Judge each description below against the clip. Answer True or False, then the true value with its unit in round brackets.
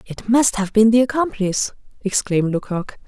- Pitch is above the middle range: True (215 Hz)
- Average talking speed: True (155 wpm)